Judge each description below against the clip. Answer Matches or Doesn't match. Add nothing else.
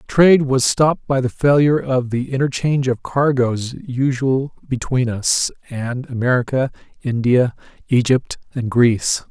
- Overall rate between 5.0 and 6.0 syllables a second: Doesn't match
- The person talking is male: Matches